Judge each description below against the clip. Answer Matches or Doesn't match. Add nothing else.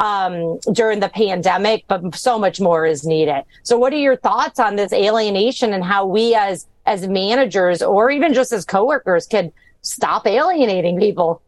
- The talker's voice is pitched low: Doesn't match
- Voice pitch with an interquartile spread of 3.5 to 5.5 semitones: Matches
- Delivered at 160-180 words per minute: Matches